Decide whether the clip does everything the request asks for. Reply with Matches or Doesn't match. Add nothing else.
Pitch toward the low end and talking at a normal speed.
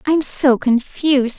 Doesn't match